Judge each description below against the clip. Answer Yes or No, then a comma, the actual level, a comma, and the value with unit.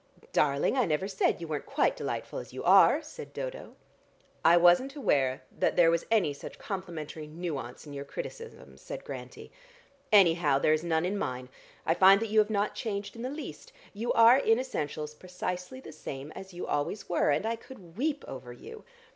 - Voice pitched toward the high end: No, medium, 180 Hz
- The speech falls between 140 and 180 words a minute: No, average, 190 wpm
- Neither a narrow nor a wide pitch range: No, wide, 7.0 semitones